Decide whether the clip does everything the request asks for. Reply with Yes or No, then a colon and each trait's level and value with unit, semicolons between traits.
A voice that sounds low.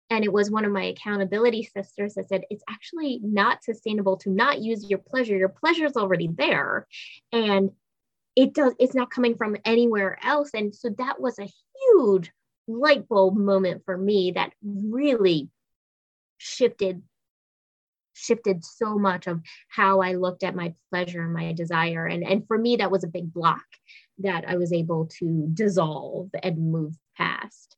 No: high, 195 Hz